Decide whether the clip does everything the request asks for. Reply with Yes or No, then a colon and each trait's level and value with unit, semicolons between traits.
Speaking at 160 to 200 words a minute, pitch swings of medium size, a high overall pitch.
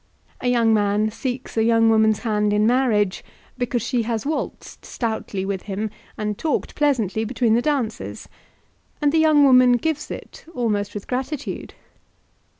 No: average, 150 wpm; average, 3.4 semitones; high, 230 Hz